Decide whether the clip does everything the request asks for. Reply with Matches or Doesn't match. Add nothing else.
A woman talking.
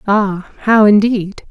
Matches